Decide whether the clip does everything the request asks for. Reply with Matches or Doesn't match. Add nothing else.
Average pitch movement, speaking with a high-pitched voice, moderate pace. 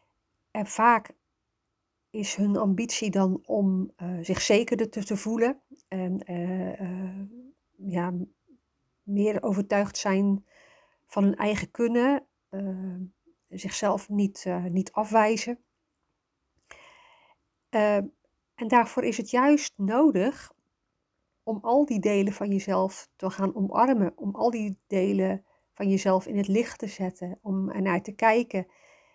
Doesn't match